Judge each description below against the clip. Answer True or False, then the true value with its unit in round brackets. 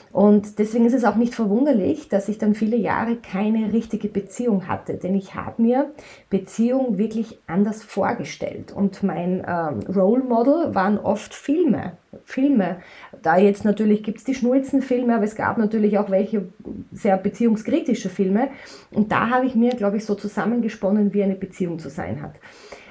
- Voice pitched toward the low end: False (210 Hz)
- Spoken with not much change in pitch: False (3.1 semitones)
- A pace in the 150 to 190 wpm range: True (170 wpm)